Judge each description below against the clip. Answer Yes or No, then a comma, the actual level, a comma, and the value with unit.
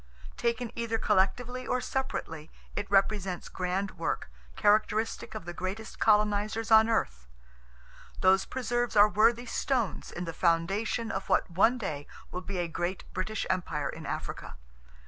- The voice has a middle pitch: No, high, 205 Hz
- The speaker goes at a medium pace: Yes, average, 150 wpm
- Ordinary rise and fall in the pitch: Yes, average, 4.0 semitones